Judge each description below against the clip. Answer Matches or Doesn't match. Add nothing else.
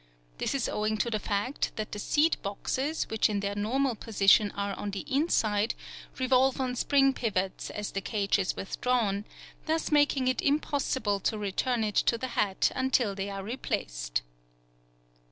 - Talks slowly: Doesn't match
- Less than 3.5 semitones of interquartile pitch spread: Doesn't match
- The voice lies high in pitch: Matches